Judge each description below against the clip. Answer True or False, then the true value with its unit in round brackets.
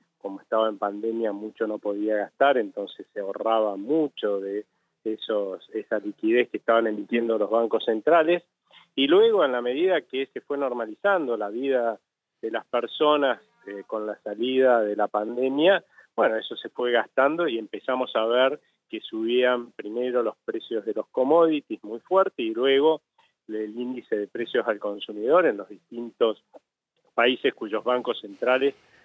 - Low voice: True (120 Hz)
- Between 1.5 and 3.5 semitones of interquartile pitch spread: False (4.5 semitones)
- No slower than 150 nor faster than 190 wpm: True (160 wpm)